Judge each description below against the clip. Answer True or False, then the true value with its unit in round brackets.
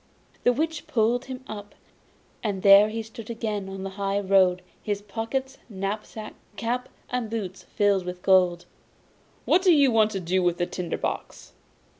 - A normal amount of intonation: True (3.2 semitones)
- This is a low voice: False (205 Hz)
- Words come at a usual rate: True (165 wpm)